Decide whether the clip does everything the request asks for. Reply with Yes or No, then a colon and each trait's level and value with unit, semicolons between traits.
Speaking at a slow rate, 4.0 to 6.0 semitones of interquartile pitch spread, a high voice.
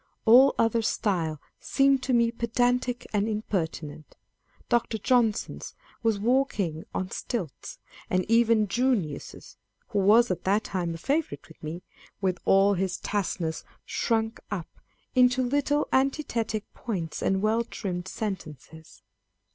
Yes: slow, 125 wpm; average, 4.8 semitones; high, 215 Hz